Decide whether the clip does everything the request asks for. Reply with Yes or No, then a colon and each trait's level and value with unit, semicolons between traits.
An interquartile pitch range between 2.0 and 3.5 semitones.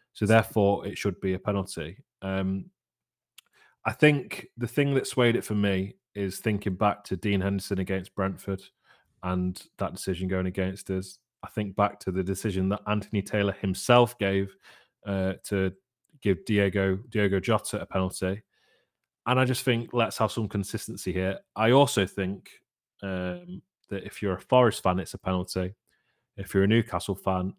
Yes: average, 2.8 semitones